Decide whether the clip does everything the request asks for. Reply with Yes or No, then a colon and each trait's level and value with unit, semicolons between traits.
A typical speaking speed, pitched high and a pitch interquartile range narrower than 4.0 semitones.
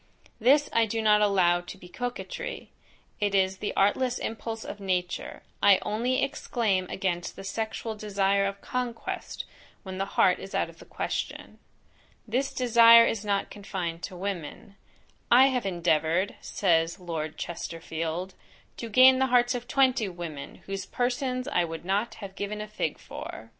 No: average, 160 wpm; high, 200 Hz; average, 4.4 semitones